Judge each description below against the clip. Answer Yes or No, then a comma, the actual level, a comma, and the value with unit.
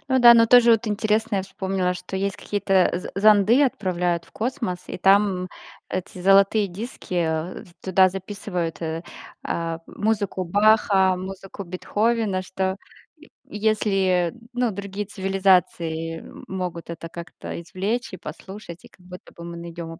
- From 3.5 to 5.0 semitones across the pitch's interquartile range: No, average, 2.7 semitones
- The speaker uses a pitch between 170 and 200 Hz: Yes, high, 190 Hz